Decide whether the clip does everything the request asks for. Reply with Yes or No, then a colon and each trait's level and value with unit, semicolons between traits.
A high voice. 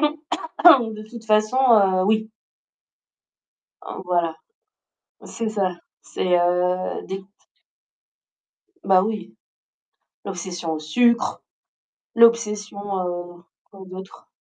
Yes: high, 200 Hz